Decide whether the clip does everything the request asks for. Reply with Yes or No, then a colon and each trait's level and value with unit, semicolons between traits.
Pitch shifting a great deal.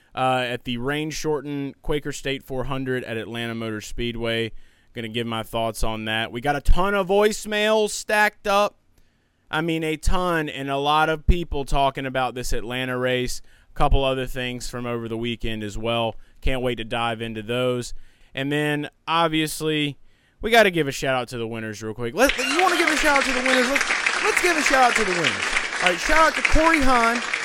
Yes: wide, 7.4 semitones